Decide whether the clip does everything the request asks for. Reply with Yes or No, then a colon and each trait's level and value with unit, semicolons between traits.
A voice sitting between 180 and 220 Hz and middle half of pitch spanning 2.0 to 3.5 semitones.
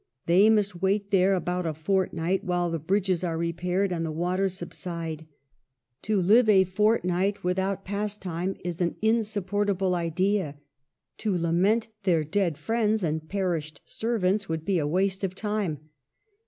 Yes: medium, 185 Hz; average, 3.1 semitones